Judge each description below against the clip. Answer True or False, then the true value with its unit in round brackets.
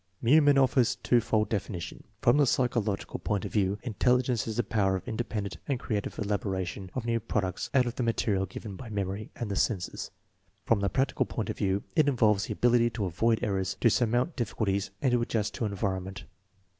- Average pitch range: True (3.6 semitones)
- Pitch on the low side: True (110 Hz)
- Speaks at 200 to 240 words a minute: True (205 wpm)